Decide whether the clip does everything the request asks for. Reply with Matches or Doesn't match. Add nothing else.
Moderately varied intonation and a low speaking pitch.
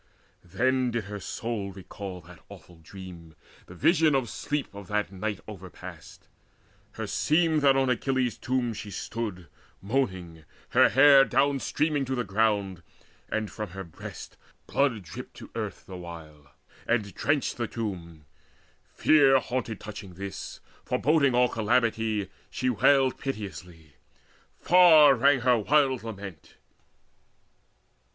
Doesn't match